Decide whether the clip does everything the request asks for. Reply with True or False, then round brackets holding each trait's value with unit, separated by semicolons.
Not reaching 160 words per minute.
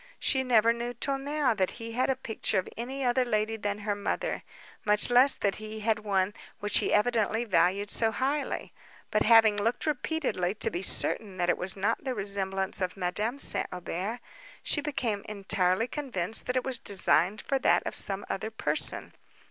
False (185 wpm)